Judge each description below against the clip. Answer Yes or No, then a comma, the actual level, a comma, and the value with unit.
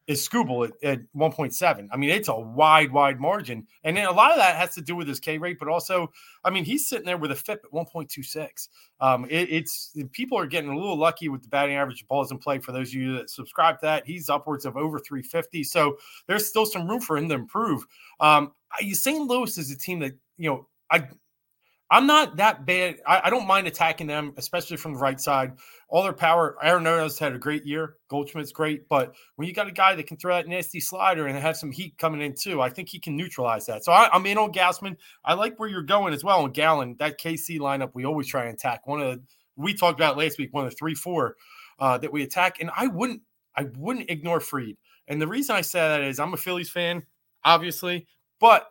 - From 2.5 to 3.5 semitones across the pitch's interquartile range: No, average, 4.0 semitones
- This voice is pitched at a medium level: Yes, medium, 160 Hz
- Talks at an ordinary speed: No, fast, 245 wpm